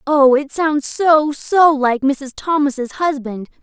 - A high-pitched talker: Yes, very high, 285 Hz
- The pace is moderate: No, slow, 115 wpm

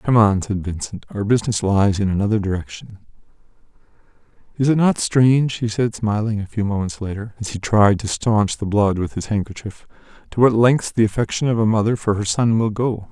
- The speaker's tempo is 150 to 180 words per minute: No, average, 200 wpm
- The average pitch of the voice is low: Yes, low, 105 Hz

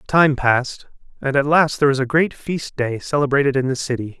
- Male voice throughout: Yes, male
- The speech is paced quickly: Yes, fast, 215 wpm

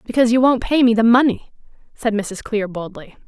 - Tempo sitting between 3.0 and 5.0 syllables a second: No, 5.6 syllables/s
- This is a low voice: No, high, 225 Hz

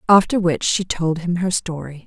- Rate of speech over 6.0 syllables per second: No, 4.8 syllables/s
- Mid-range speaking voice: Yes, medium, 175 Hz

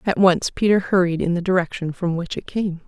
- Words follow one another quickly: Yes, fast, 230 wpm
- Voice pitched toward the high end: No, medium, 180 Hz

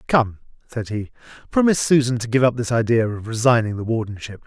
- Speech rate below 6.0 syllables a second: No, 6.1 syllables/s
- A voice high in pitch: No, low, 115 Hz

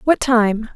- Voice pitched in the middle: No, high, 235 Hz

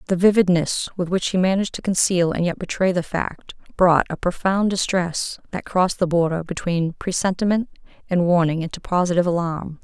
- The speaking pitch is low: No, medium, 180 Hz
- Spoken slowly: No, average, 170 wpm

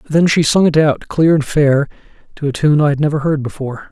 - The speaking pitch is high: No, medium, 150 Hz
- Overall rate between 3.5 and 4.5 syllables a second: No, 5.7 syllables/s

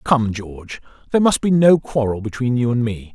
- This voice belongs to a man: Yes, male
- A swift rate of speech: Yes, fast, 210 wpm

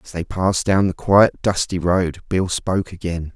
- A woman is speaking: No, male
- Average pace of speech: Yes, average, 195 wpm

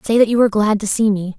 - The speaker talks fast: Yes, fast, 345 wpm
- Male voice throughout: No, female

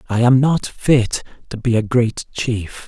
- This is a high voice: No, low, 120 Hz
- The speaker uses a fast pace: No, average, 190 wpm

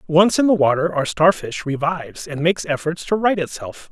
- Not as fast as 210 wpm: Yes, average, 200 wpm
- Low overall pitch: No, medium, 165 Hz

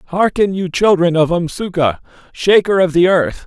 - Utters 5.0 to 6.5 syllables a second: No, 4.5 syllables/s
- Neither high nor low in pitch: Yes, medium, 175 Hz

